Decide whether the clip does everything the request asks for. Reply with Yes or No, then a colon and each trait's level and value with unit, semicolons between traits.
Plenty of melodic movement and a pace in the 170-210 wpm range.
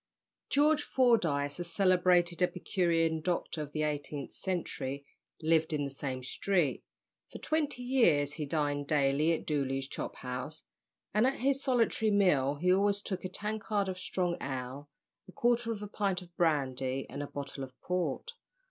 No: wide, 5.9 semitones; average, 160 wpm